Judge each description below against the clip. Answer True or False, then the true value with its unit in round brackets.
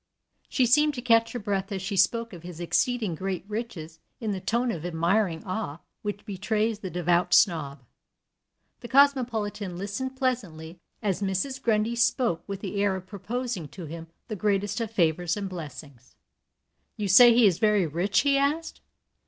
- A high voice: True (200 Hz)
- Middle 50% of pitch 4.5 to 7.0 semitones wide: True (4.8 semitones)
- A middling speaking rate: True (170 wpm)